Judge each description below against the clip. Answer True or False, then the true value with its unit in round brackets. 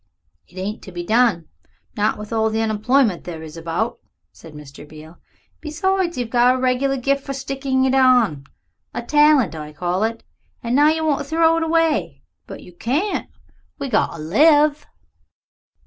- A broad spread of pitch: True (7.7 semitones)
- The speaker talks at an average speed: True (175 wpm)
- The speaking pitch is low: False (245 Hz)